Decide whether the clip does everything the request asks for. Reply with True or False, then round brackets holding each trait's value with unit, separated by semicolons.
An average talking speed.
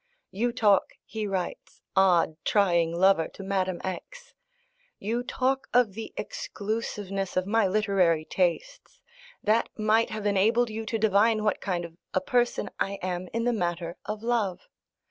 True (150 wpm)